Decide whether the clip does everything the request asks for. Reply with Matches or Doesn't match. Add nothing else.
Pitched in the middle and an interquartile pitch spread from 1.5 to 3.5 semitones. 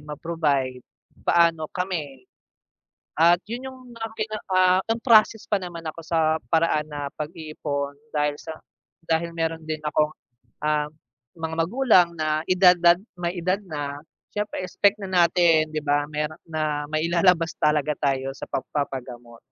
Matches